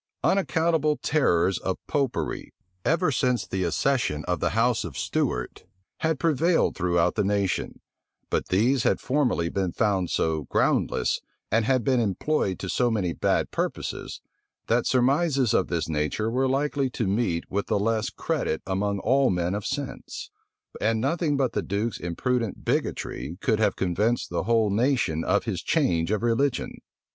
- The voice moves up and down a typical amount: No, wide, 6.1 semitones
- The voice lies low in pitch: Yes, low, 115 Hz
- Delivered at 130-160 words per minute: Yes, average, 155 wpm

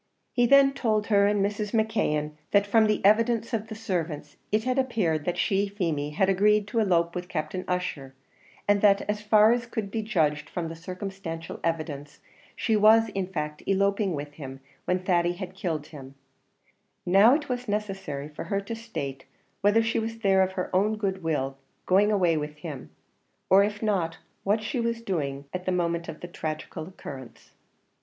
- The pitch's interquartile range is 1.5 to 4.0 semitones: No, average, 4.6 semitones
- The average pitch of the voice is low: No, high, 195 Hz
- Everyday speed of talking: Yes, average, 180 wpm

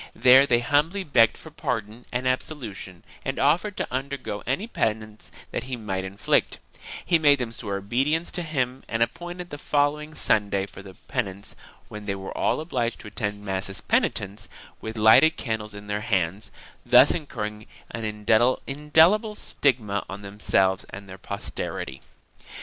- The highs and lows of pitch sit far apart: Yes, wide, 5.9 semitones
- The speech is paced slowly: No, average, 155 wpm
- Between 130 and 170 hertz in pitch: No, low, 115 Hz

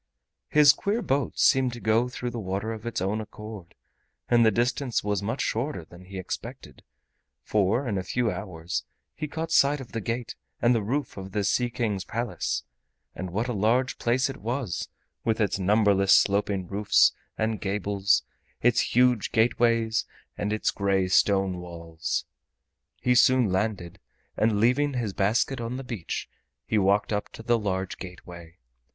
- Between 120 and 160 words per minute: No, average, 170 wpm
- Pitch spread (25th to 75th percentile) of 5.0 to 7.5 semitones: No, average, 3.8 semitones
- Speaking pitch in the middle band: No, low, 110 Hz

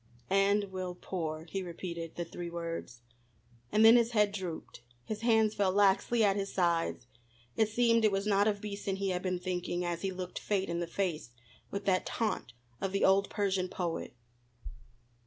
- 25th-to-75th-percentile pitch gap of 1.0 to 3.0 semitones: Yes, average, 2.7 semitones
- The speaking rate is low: No, average, 180 wpm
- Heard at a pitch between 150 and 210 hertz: Yes, high, 190 Hz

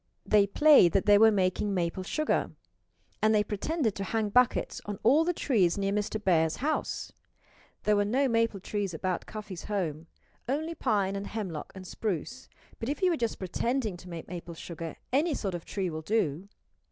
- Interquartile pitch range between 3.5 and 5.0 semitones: Yes, average, 4.1 semitones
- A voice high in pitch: Yes, high, 205 Hz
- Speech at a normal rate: Yes, average, 185 wpm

